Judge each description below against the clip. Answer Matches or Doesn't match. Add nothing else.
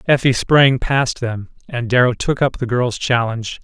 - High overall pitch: Doesn't match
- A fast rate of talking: Doesn't match